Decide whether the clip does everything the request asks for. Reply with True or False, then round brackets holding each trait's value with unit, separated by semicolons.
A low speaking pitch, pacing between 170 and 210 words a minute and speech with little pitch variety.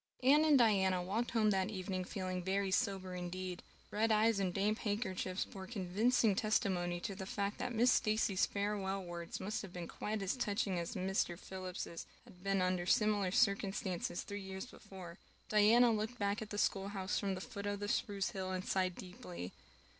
False (195 Hz; 180 wpm; 2.3 semitones)